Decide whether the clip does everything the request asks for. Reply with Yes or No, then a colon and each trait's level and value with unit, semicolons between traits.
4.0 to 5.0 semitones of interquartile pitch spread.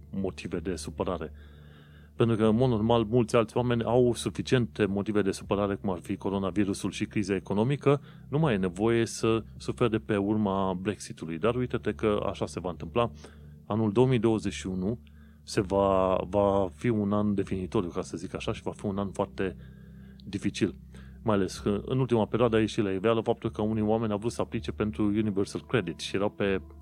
No: average, 3.3 semitones